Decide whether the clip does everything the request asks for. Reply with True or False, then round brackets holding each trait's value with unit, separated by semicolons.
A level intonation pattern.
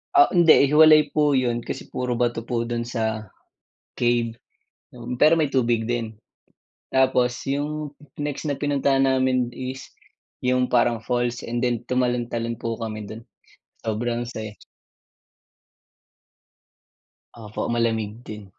True (2.3 semitones)